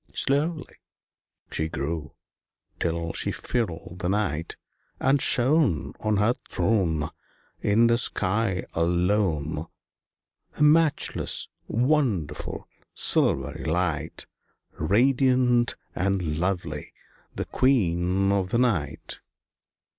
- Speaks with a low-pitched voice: Yes, very low, 95 Hz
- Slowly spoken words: Yes, slow, 90 wpm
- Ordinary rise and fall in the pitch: No, wide, 6.5 semitones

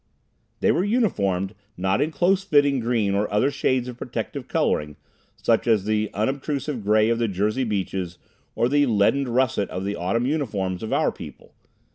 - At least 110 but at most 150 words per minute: No, average, 170 wpm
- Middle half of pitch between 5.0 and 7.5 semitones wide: Yes, wide, 5.4 semitones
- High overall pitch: No, low, 115 Hz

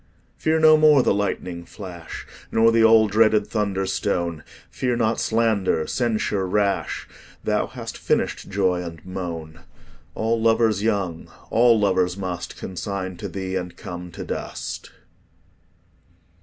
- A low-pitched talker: Yes, low, 100 Hz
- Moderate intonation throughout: Yes, average, 3.8 semitones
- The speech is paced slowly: Yes, slow, 130 wpm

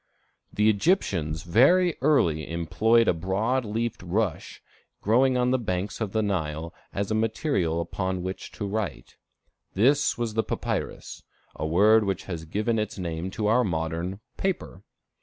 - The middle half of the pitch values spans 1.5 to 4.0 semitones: No, average, 4.8 semitones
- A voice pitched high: No, low, 100 Hz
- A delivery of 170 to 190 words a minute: No, average, 150 wpm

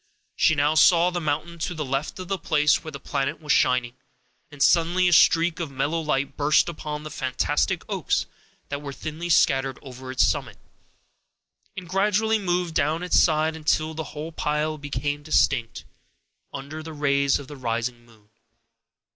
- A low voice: No, medium, 150 Hz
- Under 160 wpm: No, average, 170 wpm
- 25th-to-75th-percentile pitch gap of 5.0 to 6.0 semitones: No, average, 3.1 semitones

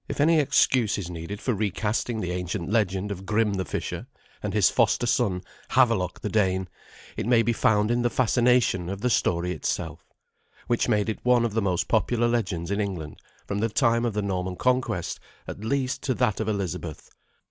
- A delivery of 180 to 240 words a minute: Yes, average, 190 wpm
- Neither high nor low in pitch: No, low, 105 Hz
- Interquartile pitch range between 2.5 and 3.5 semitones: No, average, 4.1 semitones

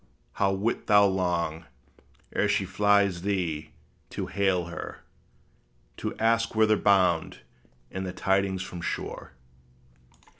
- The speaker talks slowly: Yes, slow, 115 wpm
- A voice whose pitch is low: Yes, very low, 95 Hz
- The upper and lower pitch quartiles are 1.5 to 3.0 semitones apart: Yes, narrow, 2.5 semitones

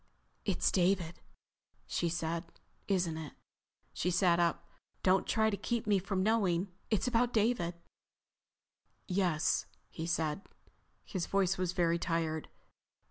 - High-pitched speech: No, medium, 180 Hz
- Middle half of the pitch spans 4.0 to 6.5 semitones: No, average, 2.8 semitones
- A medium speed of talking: No, slow, 125 wpm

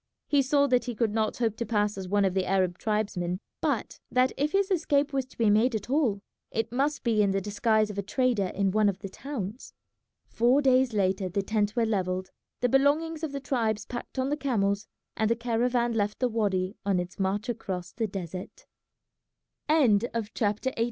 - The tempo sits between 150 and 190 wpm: No, average, 200 wpm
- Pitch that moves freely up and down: No, average, 4.2 semitones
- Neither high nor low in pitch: No, high, 220 Hz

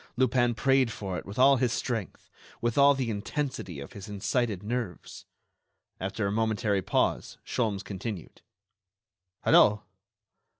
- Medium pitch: No, low, 110 Hz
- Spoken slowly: Yes, slow, 130 wpm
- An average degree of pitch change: Yes, average, 4.0 semitones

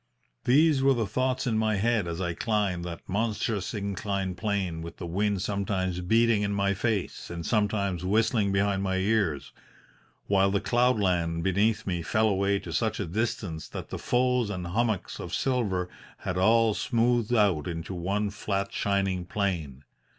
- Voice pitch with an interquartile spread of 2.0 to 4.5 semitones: Yes, average, 3.3 semitones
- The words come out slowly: No, average, 165 wpm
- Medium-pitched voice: No, low, 100 Hz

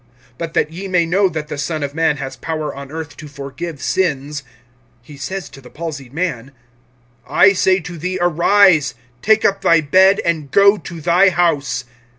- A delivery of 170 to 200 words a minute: Yes, average, 180 wpm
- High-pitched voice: No, medium, 160 Hz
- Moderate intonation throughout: Yes, average, 4.3 semitones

